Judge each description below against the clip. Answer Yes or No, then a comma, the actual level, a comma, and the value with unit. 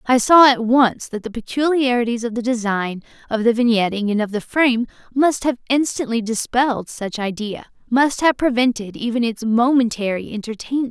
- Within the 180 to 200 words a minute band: No, average, 160 wpm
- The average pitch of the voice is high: Yes, high, 235 Hz